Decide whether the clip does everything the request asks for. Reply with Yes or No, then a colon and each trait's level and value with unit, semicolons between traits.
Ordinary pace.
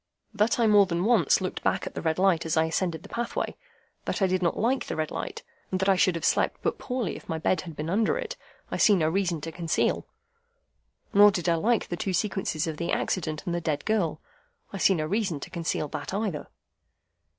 No: fast, 230 wpm